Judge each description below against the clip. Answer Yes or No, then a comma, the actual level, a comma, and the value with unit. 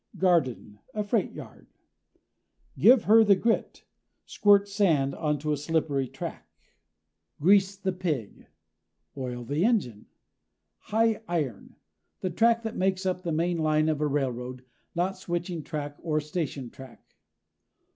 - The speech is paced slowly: Yes, slow, 130 wpm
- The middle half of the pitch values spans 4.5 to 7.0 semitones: Yes, average, 5.2 semitones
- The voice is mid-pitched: Yes, medium, 165 Hz